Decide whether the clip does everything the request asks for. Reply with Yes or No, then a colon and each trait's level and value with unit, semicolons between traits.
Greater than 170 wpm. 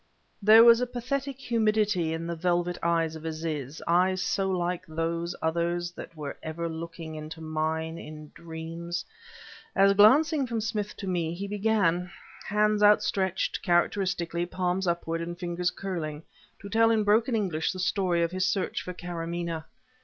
No: average, 155 wpm